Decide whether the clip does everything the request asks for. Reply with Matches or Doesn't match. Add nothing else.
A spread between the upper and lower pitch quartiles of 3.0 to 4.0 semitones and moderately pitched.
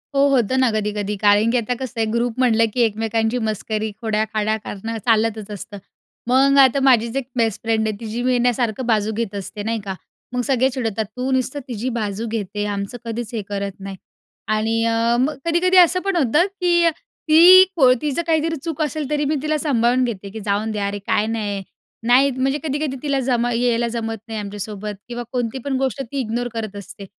Doesn't match